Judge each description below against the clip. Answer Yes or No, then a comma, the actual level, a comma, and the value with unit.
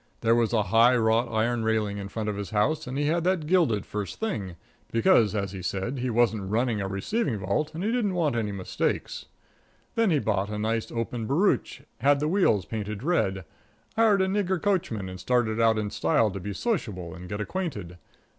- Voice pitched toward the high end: No, low, 115 Hz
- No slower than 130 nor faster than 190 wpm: No, average, 200 wpm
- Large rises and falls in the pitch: Yes, wide, 6.9 semitones